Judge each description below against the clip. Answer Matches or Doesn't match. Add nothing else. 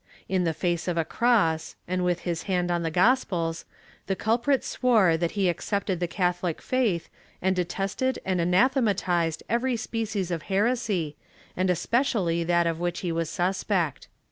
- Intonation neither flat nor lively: Matches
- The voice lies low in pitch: Doesn't match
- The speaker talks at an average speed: Matches